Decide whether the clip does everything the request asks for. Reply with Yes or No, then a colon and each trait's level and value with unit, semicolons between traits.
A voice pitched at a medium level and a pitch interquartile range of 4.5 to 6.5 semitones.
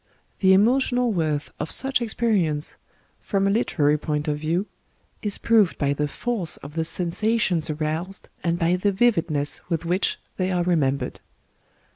Yes: medium, 175 Hz; average, 5.1 semitones